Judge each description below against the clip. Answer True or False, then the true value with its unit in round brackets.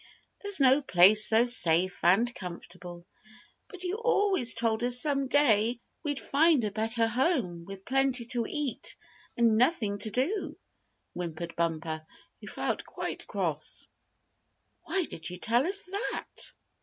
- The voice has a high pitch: True (235 Hz)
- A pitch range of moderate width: False (7.3 semitones)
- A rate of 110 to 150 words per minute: True (140 wpm)